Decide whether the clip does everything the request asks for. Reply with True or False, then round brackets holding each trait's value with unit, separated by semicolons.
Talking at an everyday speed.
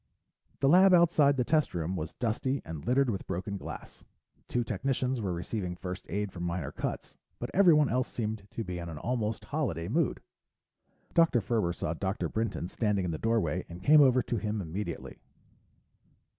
True (175 wpm)